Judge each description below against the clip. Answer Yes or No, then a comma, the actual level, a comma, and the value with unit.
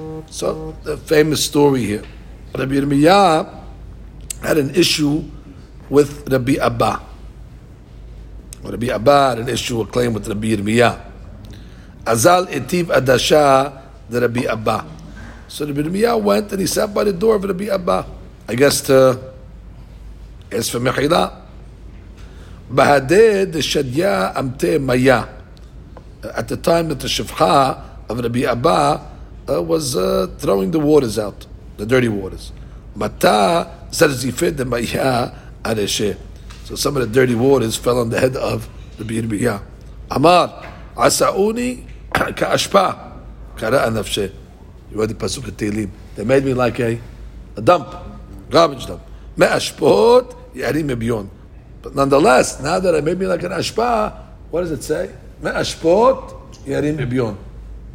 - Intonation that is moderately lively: No, wide, 5.7 semitones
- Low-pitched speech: Yes, low, 130 Hz